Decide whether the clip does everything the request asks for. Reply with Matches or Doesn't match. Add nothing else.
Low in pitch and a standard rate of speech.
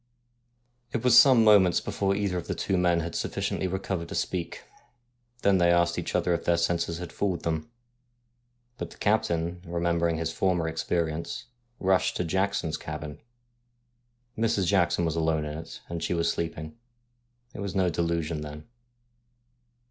Matches